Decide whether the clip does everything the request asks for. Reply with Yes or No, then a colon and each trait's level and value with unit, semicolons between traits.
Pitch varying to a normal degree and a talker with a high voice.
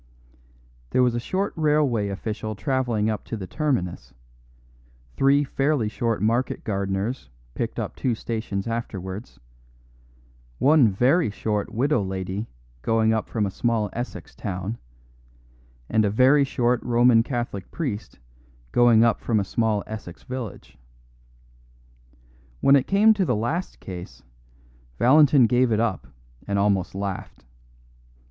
No: average, 4.1 semitones; low, 115 Hz